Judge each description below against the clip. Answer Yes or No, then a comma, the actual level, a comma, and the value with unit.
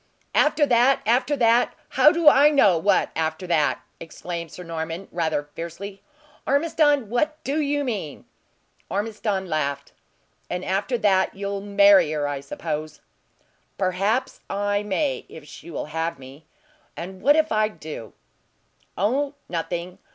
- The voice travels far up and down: Yes, wide, 7.0 semitones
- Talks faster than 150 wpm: No, slow, 135 wpm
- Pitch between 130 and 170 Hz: No, high, 195 Hz